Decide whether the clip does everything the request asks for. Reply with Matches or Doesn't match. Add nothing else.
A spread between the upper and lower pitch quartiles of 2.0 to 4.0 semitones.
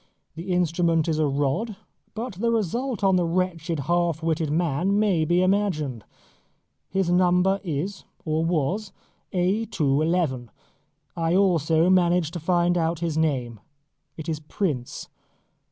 Matches